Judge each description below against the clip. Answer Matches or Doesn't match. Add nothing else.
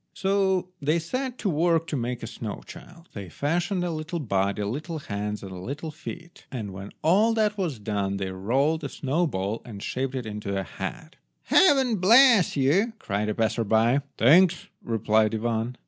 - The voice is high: Doesn't match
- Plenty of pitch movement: Matches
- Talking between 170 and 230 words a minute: Matches